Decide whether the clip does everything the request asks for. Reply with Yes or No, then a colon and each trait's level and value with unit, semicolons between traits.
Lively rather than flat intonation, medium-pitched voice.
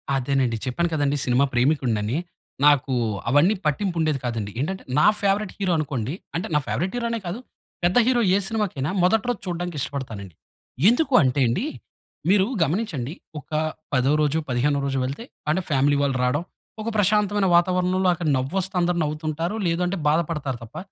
Yes: wide, 5.7 semitones; medium, 155 Hz